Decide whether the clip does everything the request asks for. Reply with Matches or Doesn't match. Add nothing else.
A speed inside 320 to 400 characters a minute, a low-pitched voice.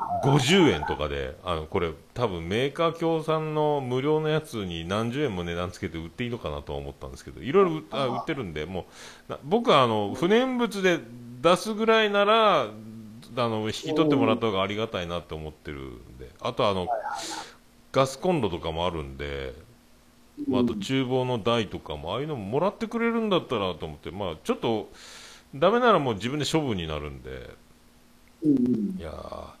Matches